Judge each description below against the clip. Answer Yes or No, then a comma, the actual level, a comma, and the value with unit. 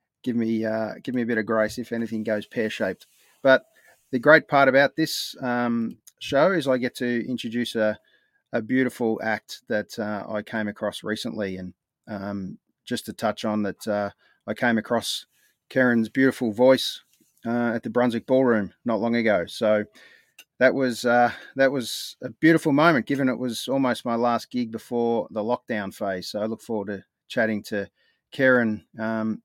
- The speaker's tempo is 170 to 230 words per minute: Yes, average, 175 wpm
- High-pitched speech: No, low, 115 Hz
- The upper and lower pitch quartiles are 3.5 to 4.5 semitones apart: No, average, 2.7 semitones